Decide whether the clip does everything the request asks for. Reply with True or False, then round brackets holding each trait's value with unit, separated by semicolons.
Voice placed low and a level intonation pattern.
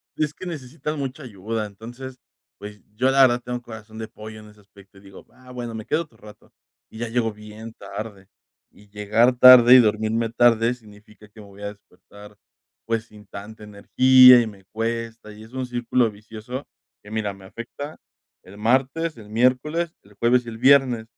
False (115 Hz; 3.1 semitones)